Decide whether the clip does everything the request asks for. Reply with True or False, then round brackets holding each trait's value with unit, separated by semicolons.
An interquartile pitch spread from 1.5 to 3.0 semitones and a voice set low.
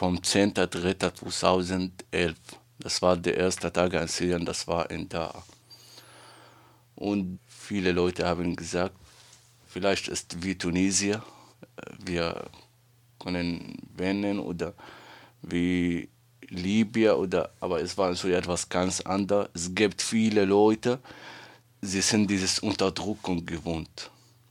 True (2.6 semitones; 95 Hz)